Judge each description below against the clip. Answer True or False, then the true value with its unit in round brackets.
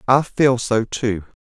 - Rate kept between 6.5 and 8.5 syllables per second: False (3.6 syllables/s)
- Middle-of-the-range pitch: False (120 Hz)